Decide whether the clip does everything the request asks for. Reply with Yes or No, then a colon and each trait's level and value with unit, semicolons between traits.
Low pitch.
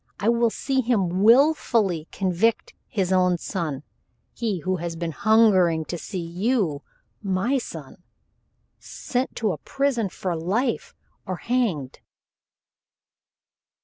No: high, 195 Hz